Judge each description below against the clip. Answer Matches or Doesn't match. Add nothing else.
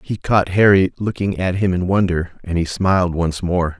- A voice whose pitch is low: Matches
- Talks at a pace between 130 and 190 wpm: Doesn't match